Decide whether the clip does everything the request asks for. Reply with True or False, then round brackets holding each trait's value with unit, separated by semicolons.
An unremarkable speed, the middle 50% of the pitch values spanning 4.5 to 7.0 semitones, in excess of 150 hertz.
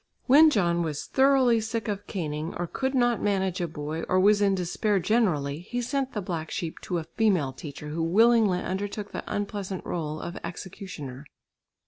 True (175 wpm; 5.0 semitones; 190 Hz)